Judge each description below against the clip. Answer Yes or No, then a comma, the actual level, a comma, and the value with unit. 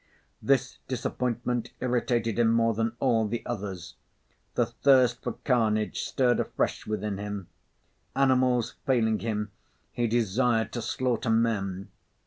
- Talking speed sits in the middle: No, slow, 120 wpm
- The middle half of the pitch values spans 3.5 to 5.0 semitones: No, narrow, 2.5 semitones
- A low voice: Yes, low, 115 Hz